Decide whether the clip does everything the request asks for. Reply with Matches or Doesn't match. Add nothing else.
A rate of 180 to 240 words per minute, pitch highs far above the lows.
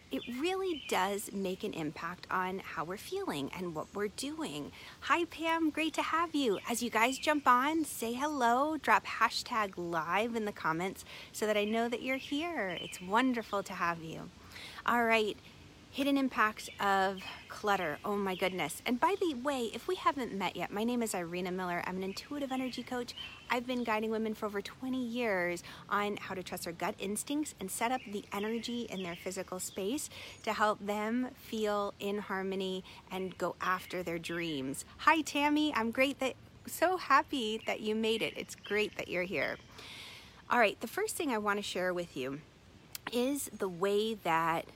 Matches